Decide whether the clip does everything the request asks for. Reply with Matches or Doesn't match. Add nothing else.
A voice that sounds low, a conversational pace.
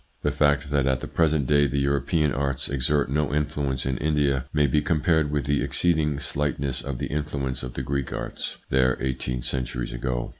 Matches